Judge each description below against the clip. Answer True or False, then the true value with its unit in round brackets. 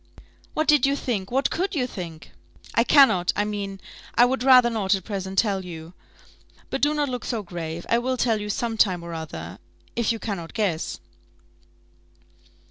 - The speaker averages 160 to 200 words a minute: True (180 wpm)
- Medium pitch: False (210 Hz)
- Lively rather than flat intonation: True (5.8 semitones)